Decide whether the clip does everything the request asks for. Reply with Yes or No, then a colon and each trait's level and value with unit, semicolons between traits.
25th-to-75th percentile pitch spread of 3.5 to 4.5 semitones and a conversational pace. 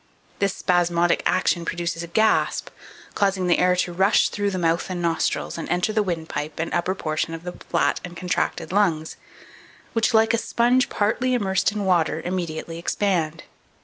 No: average, 3.1 semitones; average, 170 wpm